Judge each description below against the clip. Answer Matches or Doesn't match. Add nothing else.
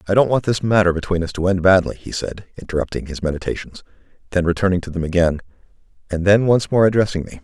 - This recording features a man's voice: Matches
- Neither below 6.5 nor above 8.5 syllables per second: Matches